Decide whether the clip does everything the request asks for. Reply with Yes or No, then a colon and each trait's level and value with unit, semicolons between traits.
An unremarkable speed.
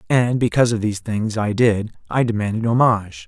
Yes: average, 185 wpm